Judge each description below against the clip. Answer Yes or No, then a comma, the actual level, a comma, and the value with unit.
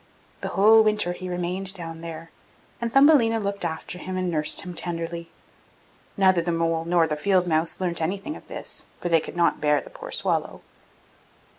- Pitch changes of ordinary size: Yes, average, 3.2 semitones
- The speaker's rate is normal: Yes, average, 180 wpm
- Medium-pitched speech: Yes, medium, 175 Hz